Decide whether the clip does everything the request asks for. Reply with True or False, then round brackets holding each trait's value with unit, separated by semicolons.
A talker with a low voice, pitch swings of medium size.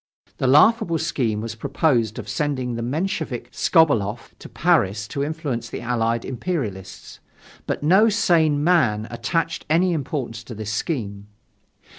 False (130 Hz; 6.0 semitones)